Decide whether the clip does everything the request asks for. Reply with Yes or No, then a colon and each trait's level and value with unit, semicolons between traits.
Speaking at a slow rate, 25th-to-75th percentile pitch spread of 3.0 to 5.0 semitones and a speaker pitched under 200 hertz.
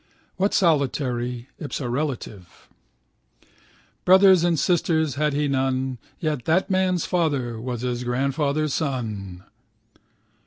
Yes: slow, 100 wpm; average, 4.5 semitones; medium, 140 Hz